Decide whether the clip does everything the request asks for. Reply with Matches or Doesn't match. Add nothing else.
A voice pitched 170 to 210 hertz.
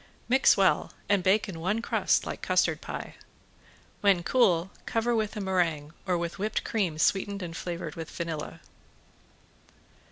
Matches